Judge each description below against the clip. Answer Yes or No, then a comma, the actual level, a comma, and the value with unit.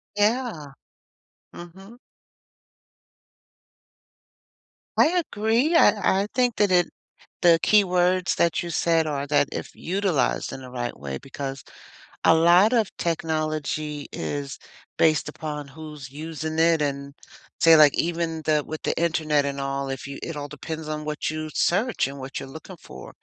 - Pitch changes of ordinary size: Yes, average, 3.6 semitones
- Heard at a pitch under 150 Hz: No, medium, 160 Hz